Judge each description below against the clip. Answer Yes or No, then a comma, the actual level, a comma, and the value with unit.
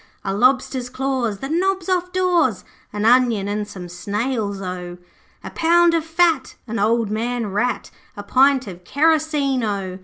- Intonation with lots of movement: Yes, wide, 7.1 semitones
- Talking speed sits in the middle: Yes, average, 155 wpm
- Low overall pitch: No, very high, 250 Hz